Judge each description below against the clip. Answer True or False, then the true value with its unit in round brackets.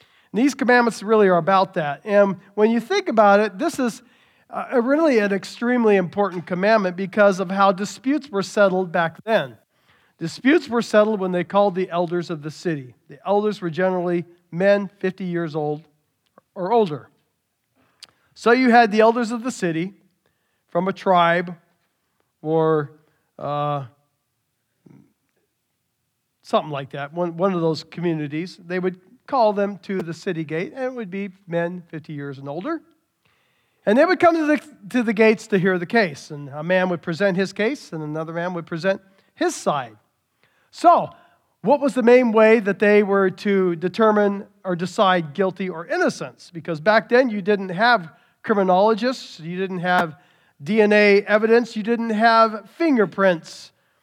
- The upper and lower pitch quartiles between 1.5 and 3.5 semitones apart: False (4.5 semitones)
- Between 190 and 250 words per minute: False (160 wpm)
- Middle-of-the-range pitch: False (195 Hz)